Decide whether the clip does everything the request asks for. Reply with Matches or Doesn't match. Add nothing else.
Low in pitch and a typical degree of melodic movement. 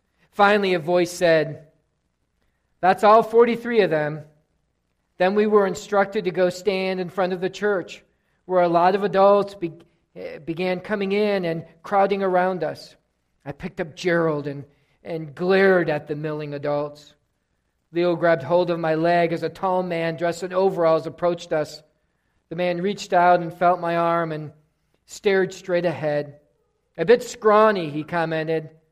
Doesn't match